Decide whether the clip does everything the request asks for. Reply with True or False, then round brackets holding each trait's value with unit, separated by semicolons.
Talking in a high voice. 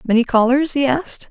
True (255 Hz)